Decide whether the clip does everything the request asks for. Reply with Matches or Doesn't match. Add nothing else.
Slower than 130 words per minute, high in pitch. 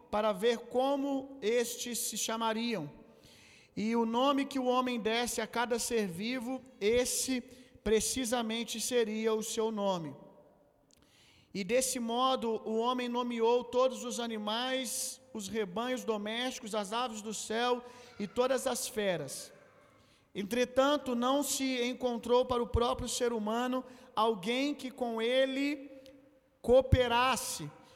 Matches